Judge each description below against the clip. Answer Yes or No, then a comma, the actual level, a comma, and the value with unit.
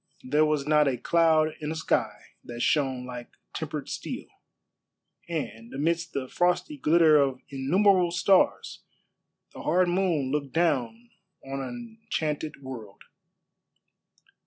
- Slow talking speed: Yes, slow, 125 wpm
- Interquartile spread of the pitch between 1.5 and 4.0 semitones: No, average, 4.5 semitones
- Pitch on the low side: No, medium, 150 Hz